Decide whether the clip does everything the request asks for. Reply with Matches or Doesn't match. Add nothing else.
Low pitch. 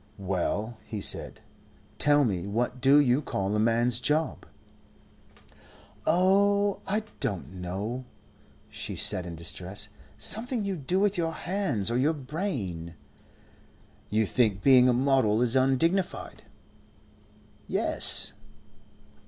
Matches